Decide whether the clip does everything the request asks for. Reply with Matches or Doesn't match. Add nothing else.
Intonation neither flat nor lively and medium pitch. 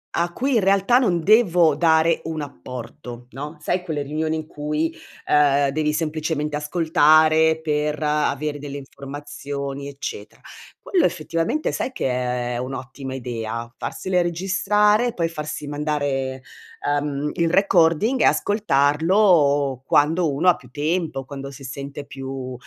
Matches